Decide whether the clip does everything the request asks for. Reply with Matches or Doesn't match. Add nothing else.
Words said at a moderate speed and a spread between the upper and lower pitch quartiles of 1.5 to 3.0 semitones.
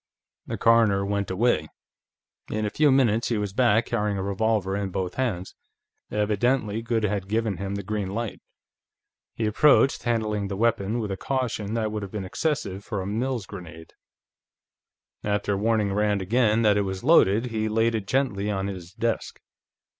Matches